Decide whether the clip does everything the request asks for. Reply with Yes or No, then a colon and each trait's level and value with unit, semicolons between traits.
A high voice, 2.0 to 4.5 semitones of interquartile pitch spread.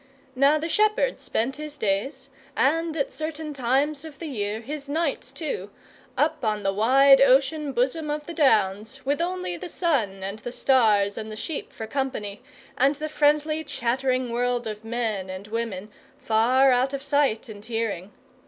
No: very high, 260 Hz; average, 5.2 semitones